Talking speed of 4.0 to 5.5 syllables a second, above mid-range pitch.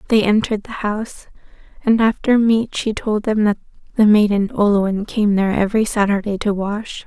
Yes: 5.3 syllables/s; high, 210 Hz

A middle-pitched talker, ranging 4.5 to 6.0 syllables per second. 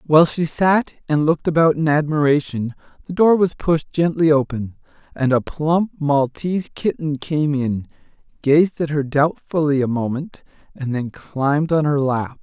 Yes: medium, 150 Hz; 4.6 syllables/s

